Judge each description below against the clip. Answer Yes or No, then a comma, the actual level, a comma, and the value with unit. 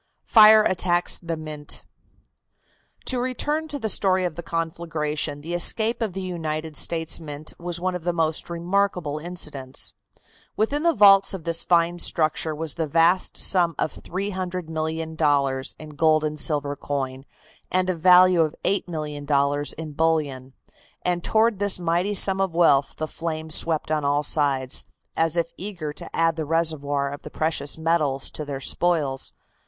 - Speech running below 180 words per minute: Yes, average, 160 wpm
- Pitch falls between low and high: Yes, medium, 165 Hz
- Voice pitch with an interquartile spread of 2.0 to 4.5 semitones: Yes, average, 3.1 semitones